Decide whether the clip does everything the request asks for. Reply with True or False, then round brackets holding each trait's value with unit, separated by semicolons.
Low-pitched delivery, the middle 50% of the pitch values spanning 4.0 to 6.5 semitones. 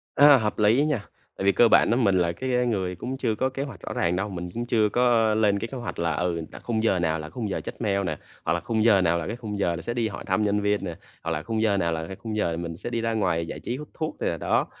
True (105 Hz; 5.0 semitones)